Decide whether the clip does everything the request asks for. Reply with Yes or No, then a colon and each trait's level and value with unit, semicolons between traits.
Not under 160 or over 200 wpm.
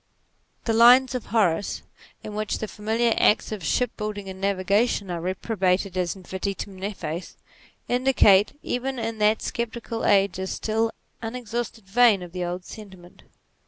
No: average, 145 wpm